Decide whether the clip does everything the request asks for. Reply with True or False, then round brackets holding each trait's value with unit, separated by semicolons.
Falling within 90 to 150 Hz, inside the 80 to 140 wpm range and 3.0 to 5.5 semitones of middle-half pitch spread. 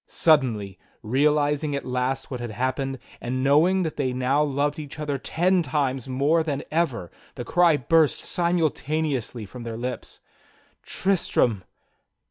True (140 Hz; 135 wpm; 3.6 semitones)